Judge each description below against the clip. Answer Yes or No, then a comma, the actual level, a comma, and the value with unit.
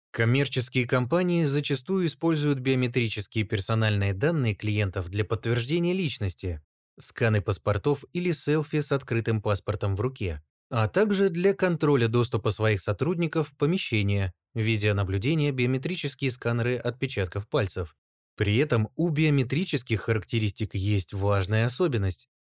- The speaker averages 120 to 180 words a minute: No, slow, 110 wpm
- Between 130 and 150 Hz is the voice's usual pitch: No, low, 115 Hz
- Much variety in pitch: Yes, wide, 5.9 semitones